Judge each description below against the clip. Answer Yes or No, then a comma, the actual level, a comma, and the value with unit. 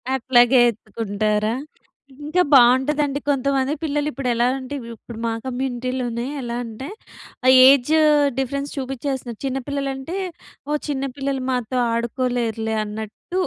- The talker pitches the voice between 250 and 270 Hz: Yes, very high, 255 Hz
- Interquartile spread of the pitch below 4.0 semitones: Yes, average, 2.8 semitones